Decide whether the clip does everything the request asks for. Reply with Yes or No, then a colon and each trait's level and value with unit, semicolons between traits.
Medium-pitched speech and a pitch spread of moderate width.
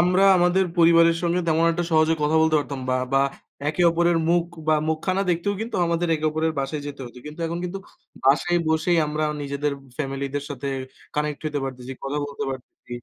Yes: medium, 155 Hz; average, 3.1 semitones